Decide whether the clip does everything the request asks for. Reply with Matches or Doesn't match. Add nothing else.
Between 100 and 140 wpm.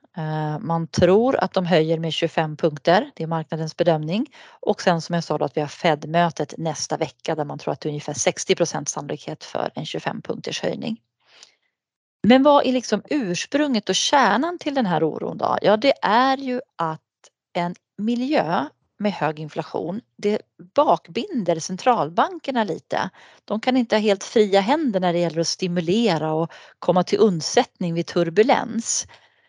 Doesn't match